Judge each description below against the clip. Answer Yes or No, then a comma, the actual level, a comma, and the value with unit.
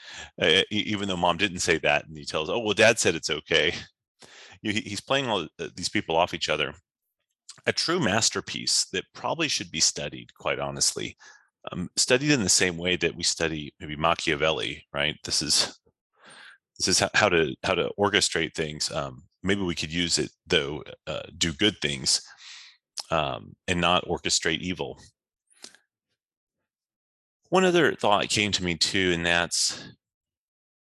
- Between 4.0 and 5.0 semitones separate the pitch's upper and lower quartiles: Yes, average, 4.5 semitones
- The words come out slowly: No, average, 155 wpm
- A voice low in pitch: Yes, very low, 85 Hz